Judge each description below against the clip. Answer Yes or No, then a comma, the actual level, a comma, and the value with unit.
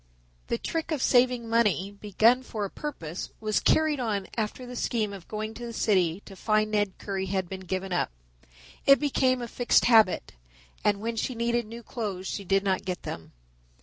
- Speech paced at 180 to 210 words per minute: Yes, average, 190 wpm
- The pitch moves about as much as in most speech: Yes, average, 3.7 semitones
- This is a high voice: Yes, high, 215 Hz